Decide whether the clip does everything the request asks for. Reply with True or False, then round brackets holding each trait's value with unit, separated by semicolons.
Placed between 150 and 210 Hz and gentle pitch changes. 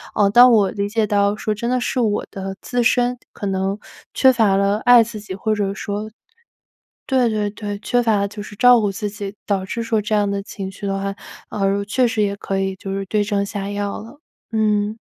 True (205 Hz; 2.0 semitones)